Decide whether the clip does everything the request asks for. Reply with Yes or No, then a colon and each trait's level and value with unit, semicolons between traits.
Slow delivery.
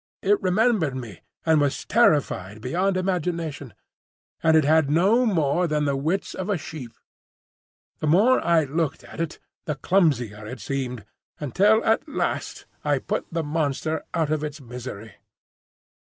No: average, 150 wpm